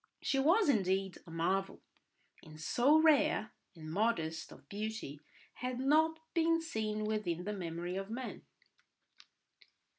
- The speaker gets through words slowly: Yes, slow, 125 wpm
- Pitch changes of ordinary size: No, wide, 7.5 semitones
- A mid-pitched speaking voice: No, high, 215 Hz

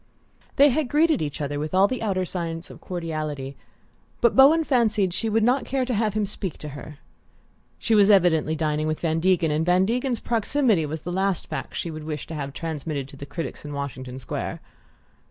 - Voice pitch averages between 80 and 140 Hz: No, medium, 175 Hz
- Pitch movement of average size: No, wide, 6.5 semitones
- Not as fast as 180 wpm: No, fast, 205 wpm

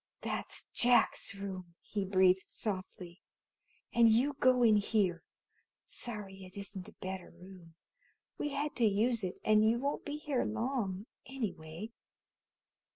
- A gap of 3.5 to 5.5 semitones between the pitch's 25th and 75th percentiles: Yes, average, 4.2 semitones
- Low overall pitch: No, high, 210 Hz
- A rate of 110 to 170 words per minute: Yes, slow, 135 wpm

